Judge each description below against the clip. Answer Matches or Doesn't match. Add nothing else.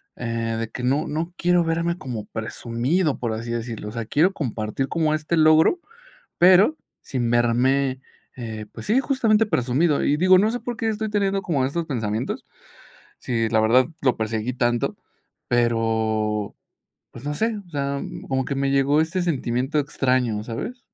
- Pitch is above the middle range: Doesn't match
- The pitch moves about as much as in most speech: Doesn't match